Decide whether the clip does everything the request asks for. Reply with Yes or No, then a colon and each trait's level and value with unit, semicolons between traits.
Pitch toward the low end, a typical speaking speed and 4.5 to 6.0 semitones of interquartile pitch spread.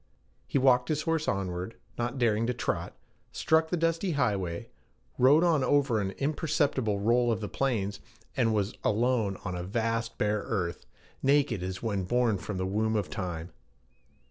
Yes: low, 115 Hz; average, 165 wpm; average, 5.3 semitones